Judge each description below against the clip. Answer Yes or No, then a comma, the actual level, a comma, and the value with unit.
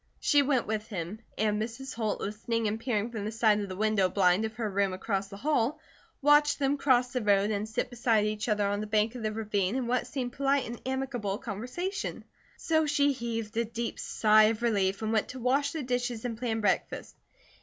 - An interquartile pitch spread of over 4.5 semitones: No, average, 3.1 semitones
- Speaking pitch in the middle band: No, high, 225 Hz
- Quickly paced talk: Yes, fast, 215 wpm